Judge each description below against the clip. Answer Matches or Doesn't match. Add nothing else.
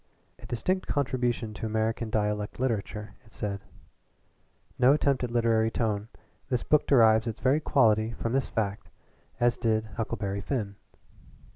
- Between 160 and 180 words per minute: Doesn't match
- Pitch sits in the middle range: Doesn't match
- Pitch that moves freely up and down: Doesn't match